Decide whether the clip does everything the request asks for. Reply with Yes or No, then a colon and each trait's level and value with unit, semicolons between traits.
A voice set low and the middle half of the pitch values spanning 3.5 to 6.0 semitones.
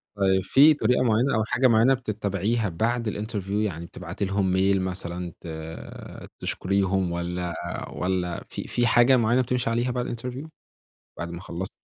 Yes: low, 100 Hz; average, 4.8 semitones